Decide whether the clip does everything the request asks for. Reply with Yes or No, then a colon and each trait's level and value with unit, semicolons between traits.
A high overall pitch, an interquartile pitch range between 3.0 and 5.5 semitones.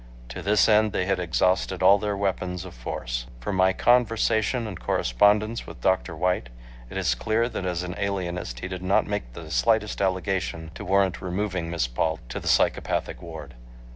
No: very low, 95 Hz; average, 3.5 semitones